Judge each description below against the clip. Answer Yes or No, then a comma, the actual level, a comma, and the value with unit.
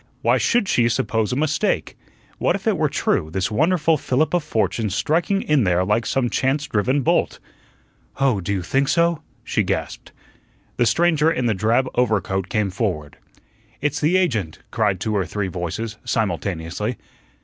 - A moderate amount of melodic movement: No, wide, 7.0 semitones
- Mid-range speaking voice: No, low, 115 Hz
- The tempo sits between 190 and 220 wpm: No, average, 165 wpm